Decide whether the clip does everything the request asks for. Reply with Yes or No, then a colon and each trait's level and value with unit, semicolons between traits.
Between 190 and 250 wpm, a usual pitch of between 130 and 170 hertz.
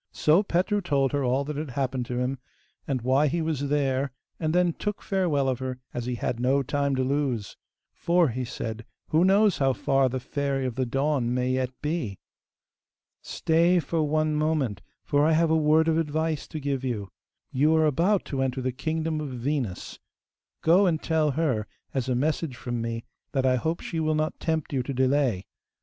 Yes: average, 200 wpm; medium, 140 Hz